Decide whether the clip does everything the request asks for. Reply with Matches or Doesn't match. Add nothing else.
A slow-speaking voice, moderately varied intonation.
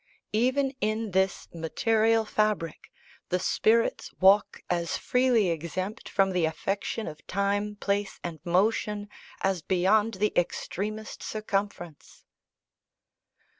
Matches